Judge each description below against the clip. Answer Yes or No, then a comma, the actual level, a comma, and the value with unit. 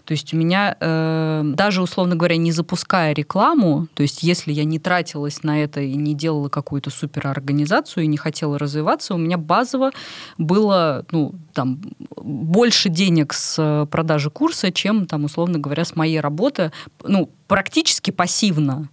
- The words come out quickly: No, average, 150 wpm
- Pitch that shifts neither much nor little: Yes, average, 3.6 semitones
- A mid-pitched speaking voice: Yes, medium, 160 Hz